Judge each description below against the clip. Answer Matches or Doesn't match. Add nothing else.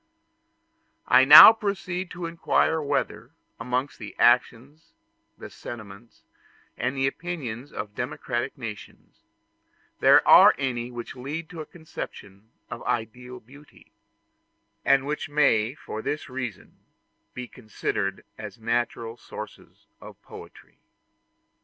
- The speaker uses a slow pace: Matches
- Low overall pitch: Matches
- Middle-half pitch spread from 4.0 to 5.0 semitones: Matches